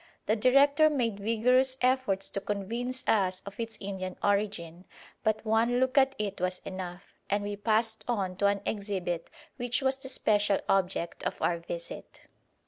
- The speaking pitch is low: No, high, 210 Hz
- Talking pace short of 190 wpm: Yes, average, 160 wpm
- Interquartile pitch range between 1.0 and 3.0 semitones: No, average, 4.2 semitones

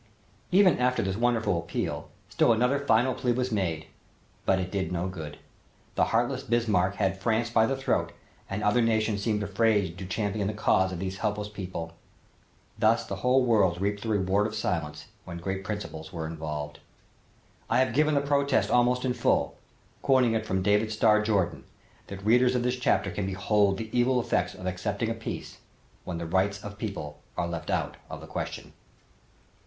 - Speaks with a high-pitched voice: No, low, 105 Hz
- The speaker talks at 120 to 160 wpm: No, average, 180 wpm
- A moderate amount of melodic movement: Yes, average, 4.0 semitones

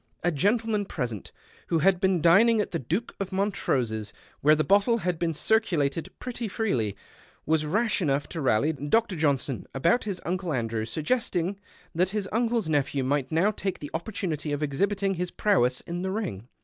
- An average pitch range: No, wide, 5.8 semitones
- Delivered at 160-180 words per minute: Yes, average, 175 wpm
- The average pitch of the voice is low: No, medium, 175 Hz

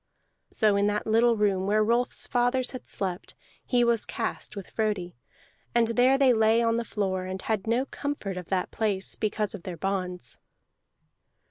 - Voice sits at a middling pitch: No, high, 215 Hz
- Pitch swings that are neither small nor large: Yes, average, 3.6 semitones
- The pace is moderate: Yes, average, 170 wpm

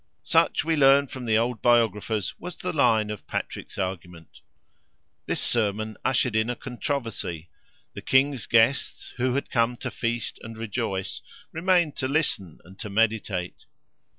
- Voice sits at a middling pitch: No, low, 115 Hz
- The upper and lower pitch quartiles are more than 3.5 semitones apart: Yes, average, 4.1 semitones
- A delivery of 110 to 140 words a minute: No, average, 150 wpm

